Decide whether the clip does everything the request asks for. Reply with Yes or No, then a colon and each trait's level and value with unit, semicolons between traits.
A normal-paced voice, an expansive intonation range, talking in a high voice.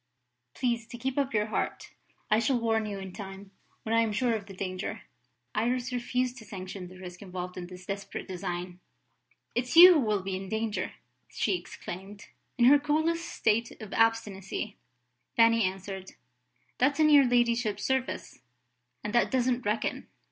No: average, 165 wpm; average, 4.3 semitones; high, 220 Hz